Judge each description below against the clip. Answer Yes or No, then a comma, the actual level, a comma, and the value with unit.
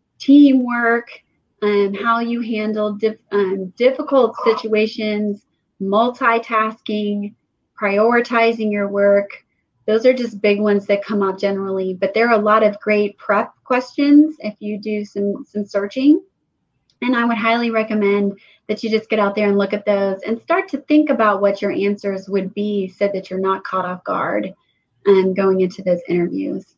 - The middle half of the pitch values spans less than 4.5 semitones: Yes, narrow, 2.5 semitones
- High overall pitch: Yes, high, 210 Hz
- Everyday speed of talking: Yes, average, 170 wpm